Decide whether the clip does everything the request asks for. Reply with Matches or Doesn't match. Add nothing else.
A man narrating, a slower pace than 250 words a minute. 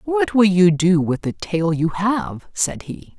Doesn't match